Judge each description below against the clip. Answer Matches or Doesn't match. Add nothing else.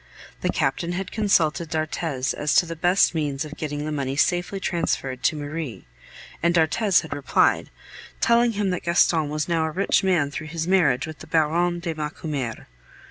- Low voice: Doesn't match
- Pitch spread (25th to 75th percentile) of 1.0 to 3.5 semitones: Matches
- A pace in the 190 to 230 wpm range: Doesn't match